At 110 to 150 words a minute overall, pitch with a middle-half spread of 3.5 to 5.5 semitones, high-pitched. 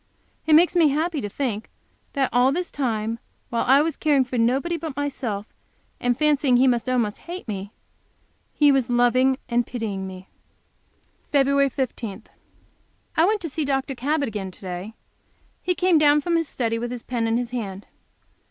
No: average, 180 wpm; average, 4.3 semitones; very high, 255 Hz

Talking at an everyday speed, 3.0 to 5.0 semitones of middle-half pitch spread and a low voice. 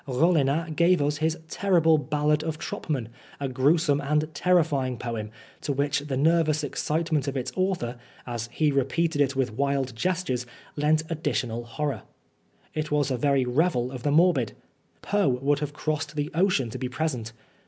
No: average, 165 wpm; average, 3.5 semitones; medium, 145 Hz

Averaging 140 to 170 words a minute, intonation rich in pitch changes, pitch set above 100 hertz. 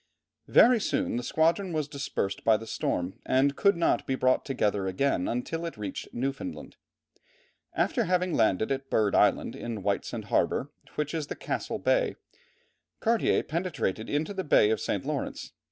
Yes: average, 160 wpm; wide, 7.4 semitones; medium, 140 Hz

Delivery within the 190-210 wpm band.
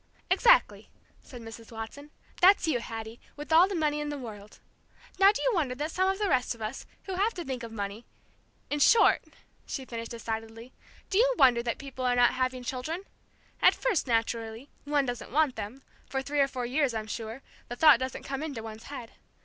Yes: fast, 205 wpm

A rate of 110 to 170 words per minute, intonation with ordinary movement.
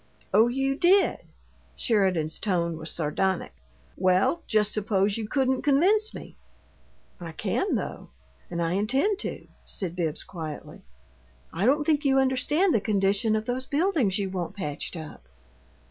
No: average, 145 wpm; wide, 6.9 semitones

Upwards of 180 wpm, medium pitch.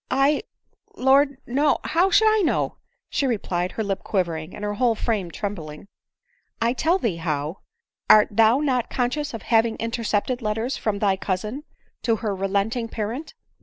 No: average, 190 wpm; high, 225 Hz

